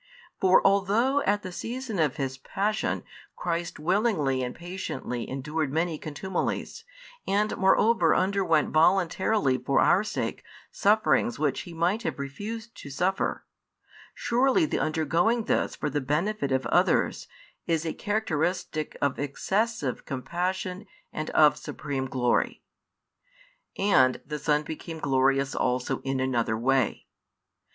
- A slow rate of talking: Yes, slow, 125 wpm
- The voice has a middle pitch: Yes, medium, 165 Hz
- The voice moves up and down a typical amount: No, wide, 6.5 semitones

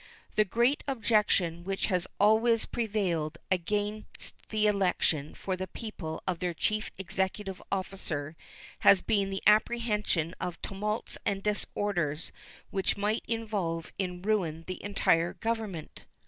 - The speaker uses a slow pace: Yes, slow, 125 wpm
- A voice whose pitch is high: Yes, high, 195 Hz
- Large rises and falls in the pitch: No, average, 3.4 semitones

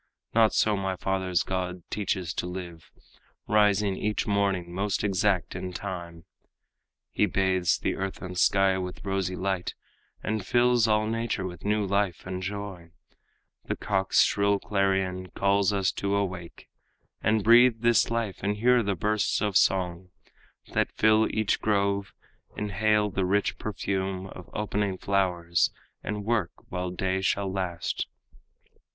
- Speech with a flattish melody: Yes, narrow, 2.1 semitones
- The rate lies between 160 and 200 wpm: No, average, 140 wpm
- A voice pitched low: Yes, very low, 95 Hz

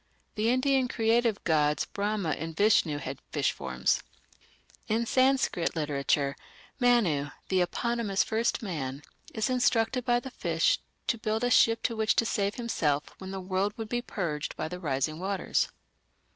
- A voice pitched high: Yes, high, 205 Hz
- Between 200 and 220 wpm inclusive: No, average, 155 wpm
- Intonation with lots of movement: Yes, wide, 6.9 semitones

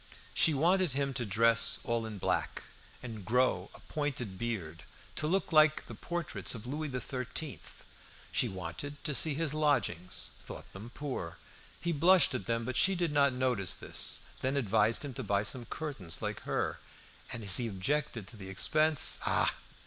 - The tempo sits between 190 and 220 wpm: No, average, 170 wpm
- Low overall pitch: Yes, low, 125 Hz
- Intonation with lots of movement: Yes, wide, 5.8 semitones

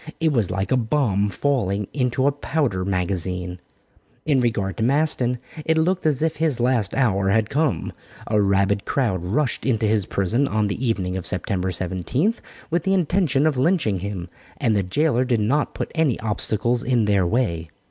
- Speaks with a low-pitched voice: Yes, low, 115 Hz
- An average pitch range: No, wide, 6.4 semitones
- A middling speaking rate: Yes, average, 180 wpm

